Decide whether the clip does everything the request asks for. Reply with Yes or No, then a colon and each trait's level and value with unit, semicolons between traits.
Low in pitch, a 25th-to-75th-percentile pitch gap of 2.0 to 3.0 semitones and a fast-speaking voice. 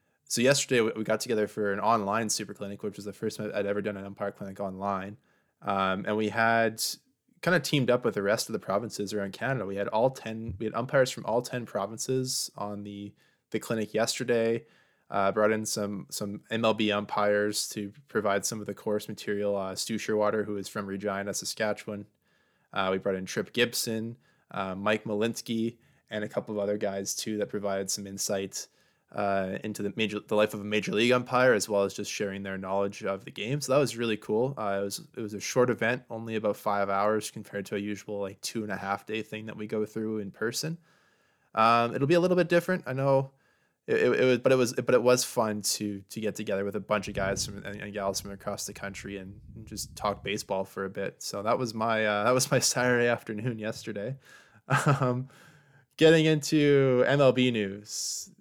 Yes: low, 105 Hz; average, 2.7 semitones; fast, 220 wpm